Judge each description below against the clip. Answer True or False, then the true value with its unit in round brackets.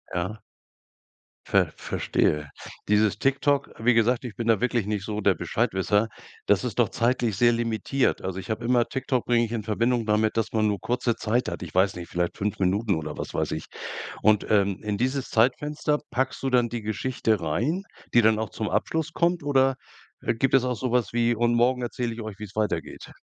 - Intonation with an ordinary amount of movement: True (3.0 semitones)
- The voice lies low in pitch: True (115 Hz)